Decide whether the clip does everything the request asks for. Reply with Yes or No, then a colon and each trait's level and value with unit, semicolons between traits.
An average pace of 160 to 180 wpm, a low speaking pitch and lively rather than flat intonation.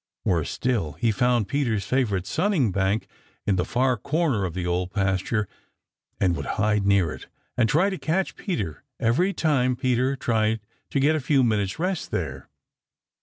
Yes: average, 170 wpm; low, 115 Hz; wide, 6.0 semitones